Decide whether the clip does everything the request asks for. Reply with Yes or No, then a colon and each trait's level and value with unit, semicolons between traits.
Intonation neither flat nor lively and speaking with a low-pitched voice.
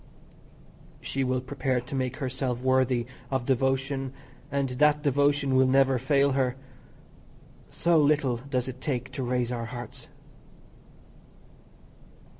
No: narrow, 1.5 semitones; low, 130 Hz